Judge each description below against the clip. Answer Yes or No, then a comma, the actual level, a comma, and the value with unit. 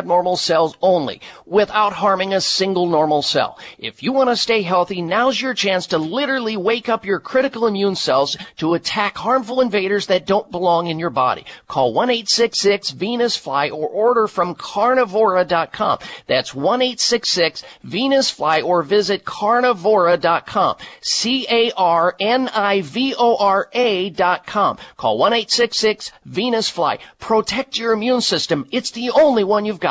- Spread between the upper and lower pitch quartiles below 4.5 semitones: No, average, 4.8 semitones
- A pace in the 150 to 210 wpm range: No, average, 140 wpm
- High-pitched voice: Yes, high, 205 Hz